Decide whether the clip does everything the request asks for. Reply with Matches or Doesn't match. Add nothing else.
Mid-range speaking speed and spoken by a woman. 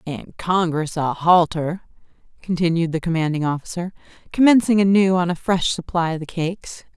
Matches